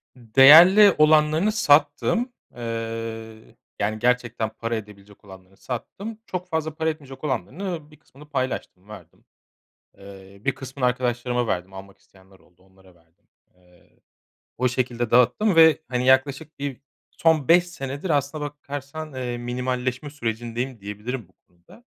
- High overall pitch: No, low, 125 Hz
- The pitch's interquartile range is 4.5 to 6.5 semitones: Yes, average, 5.3 semitones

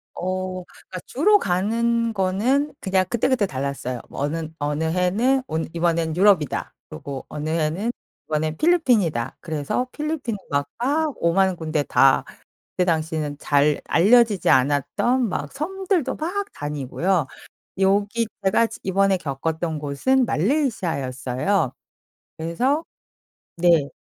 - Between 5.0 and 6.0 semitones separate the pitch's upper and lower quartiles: No, wide, 7.4 semitones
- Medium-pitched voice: Yes, medium, 180 Hz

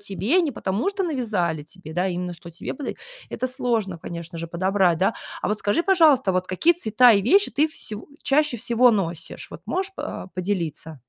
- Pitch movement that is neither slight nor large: No, wide, 7.4 semitones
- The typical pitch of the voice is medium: No, high, 205 Hz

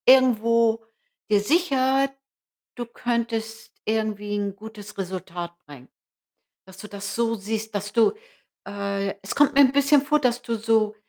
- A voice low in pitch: No, high, 220 Hz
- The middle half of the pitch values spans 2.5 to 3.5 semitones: Yes, average, 3.2 semitones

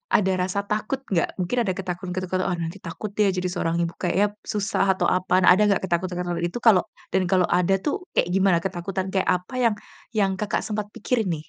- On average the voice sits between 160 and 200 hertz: Yes, medium, 185 Hz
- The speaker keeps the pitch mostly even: Yes, narrow, 2.3 semitones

